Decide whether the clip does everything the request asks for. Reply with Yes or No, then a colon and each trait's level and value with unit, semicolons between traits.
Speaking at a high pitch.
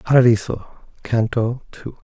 No: low, 115 Hz